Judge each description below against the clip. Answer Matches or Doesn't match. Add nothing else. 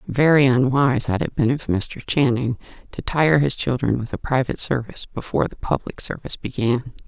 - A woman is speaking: Matches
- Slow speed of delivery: Doesn't match